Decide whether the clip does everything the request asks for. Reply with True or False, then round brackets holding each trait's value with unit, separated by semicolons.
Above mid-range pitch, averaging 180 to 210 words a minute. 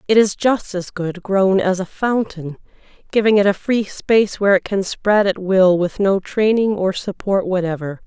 True (195 Hz; 195 wpm)